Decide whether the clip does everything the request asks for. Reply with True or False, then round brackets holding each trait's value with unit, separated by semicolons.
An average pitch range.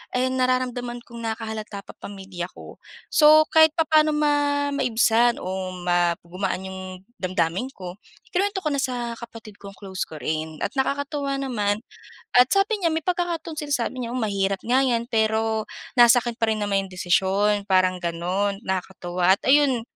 False (5.8 semitones)